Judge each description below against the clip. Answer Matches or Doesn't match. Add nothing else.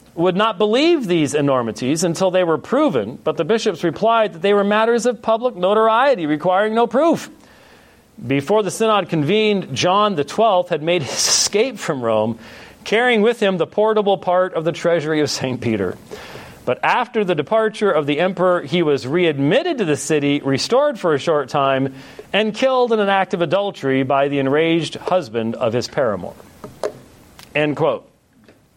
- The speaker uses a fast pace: Doesn't match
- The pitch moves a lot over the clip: Matches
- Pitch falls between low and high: Matches